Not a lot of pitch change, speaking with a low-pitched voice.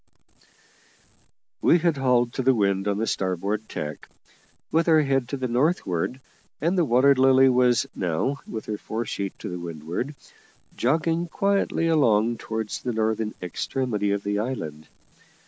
No: average, 5.2 semitones; low, 120 Hz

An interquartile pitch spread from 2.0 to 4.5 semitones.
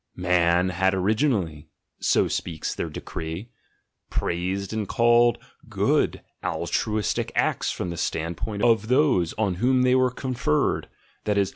No: average, 5.2 semitones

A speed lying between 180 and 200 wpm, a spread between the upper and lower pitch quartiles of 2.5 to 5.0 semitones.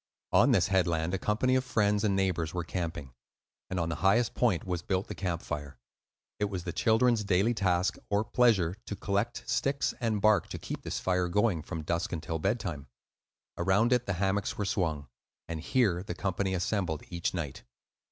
Yes: average, 185 wpm; average, 3.7 semitones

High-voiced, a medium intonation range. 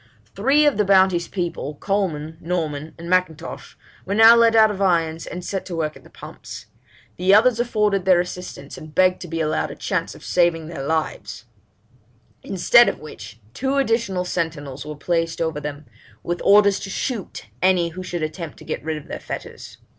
No: medium, 175 Hz; average, 3.9 semitones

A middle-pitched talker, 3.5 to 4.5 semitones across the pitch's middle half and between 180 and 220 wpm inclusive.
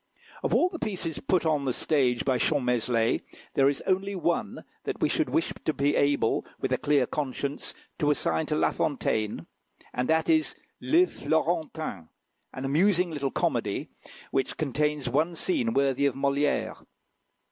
No: medium, 145 Hz; average, 4.2 semitones; average, 160 wpm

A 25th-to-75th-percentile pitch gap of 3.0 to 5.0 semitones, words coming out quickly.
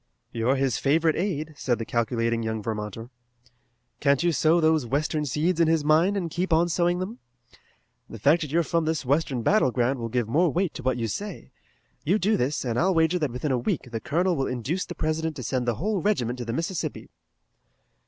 No: wide, 5.6 semitones; fast, 215 wpm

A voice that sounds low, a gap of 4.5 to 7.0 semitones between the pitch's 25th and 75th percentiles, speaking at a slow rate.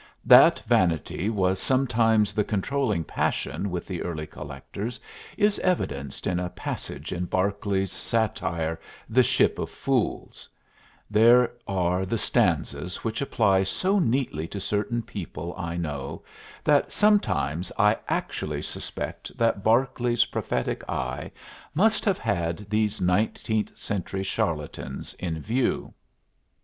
Yes: low, 100 Hz; average, 5.0 semitones; slow, 120 wpm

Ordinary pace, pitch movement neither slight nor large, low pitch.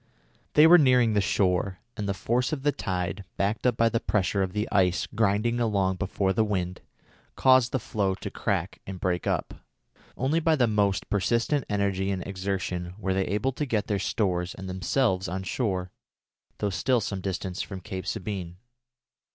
Yes: average, 180 wpm; average, 3.6 semitones; low, 100 Hz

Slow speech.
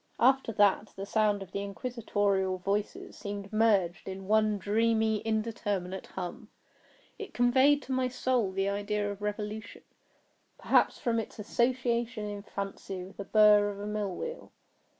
No: average, 145 wpm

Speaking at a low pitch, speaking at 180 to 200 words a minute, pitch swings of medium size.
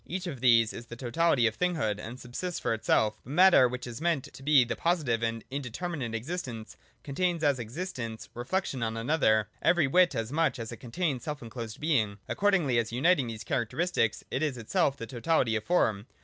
No: low, 130 Hz; average, 190 wpm; wide, 6.2 semitones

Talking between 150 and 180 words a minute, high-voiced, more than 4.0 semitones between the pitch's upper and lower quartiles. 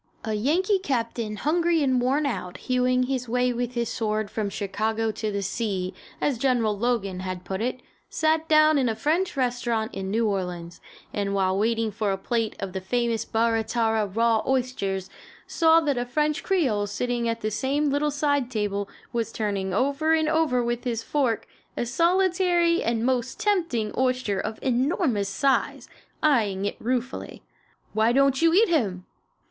Yes: average, 170 wpm; high, 240 Hz; average, 4.7 semitones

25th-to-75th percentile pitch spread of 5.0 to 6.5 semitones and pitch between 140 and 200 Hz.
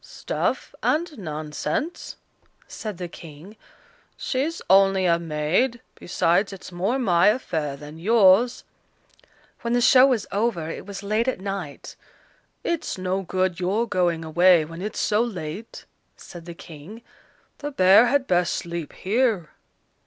Yes: average, 5.3 semitones; high, 190 Hz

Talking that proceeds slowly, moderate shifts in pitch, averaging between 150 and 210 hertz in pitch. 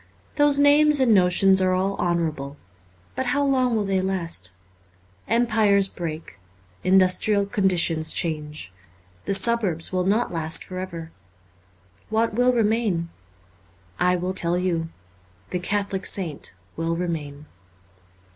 Yes: slow, 125 wpm; average, 4.4 semitones; medium, 185 Hz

